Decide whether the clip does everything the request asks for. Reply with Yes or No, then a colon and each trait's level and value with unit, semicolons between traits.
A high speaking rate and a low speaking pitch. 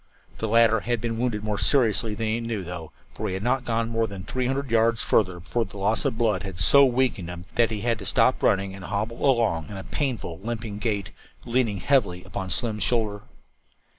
Yes: fast, 215 wpm; low, 110 Hz